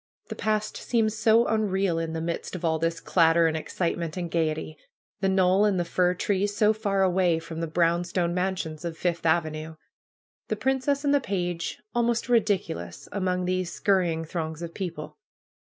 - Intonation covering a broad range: No, average, 3.5 semitones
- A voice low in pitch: No, medium, 180 Hz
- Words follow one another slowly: No, average, 175 wpm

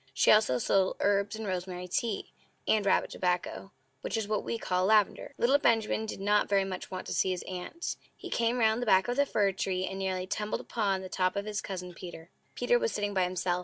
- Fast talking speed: Yes, fast, 225 wpm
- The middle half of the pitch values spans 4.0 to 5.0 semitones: No, average, 2.8 semitones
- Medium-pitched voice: No, high, 195 Hz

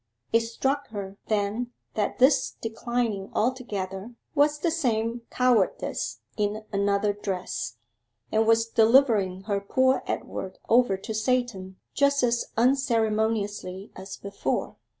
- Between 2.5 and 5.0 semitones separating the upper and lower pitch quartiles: Yes, average, 3.6 semitones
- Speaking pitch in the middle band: No, high, 220 Hz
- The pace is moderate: No, slow, 115 wpm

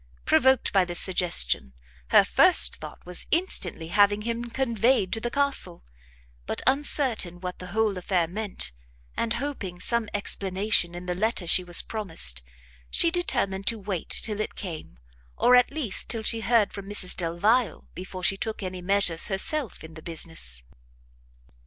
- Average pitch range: Yes, average, 4.7 semitones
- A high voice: Yes, high, 200 Hz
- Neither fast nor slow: Yes, average, 160 wpm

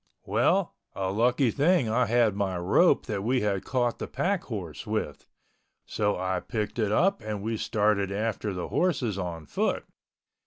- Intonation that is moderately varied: Yes, average, 3.8 semitones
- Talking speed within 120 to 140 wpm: No, average, 165 wpm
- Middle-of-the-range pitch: No, low, 110 Hz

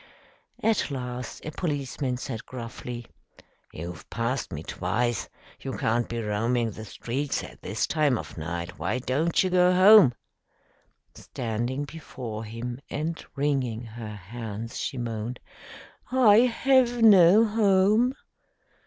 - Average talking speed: No, slow, 125 wpm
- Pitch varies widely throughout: Yes, wide, 7.1 semitones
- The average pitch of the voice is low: Yes, low, 125 Hz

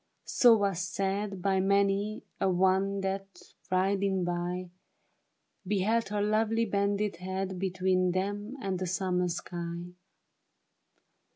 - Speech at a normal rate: No, slow, 110 wpm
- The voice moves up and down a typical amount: No, narrow, 1.5 semitones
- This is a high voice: Yes, high, 195 Hz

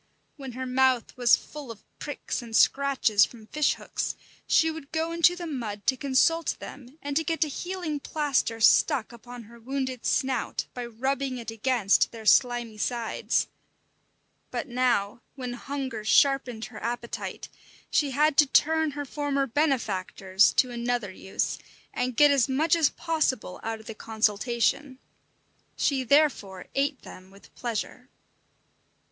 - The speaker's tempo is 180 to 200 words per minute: No, average, 150 wpm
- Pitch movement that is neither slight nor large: Yes, average, 3.8 semitones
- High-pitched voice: Yes, very high, 255 Hz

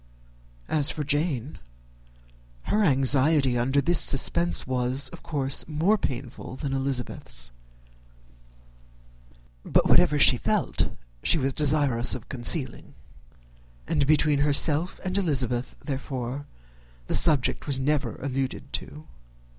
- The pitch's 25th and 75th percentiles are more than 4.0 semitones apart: No, average, 2.7 semitones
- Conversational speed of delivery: No, slow, 110 wpm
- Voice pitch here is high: No, medium, 140 Hz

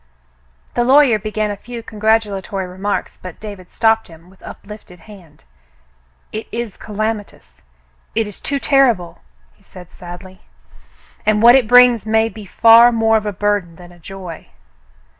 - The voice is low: No, high, 210 Hz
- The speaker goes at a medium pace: Yes, average, 150 wpm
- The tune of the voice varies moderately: Yes, average, 3.2 semitones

